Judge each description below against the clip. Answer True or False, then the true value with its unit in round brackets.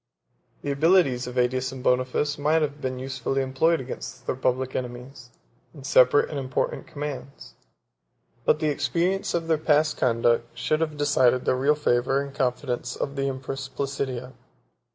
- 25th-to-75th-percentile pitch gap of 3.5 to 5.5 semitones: False (2.5 semitones)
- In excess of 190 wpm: False (155 wpm)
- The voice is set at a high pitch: False (135 Hz)